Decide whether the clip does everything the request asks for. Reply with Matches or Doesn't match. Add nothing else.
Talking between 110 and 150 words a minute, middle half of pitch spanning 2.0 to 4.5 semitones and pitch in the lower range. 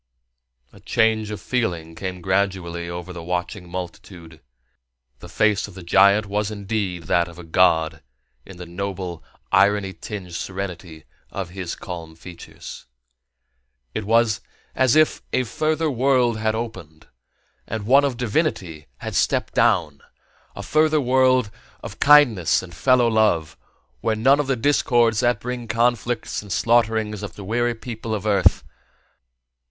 Doesn't match